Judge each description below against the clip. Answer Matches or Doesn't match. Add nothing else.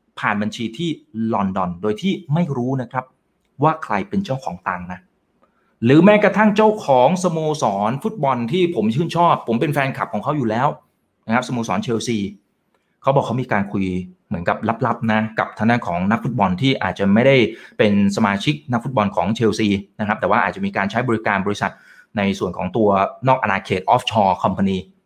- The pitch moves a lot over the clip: Matches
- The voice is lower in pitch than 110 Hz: Doesn't match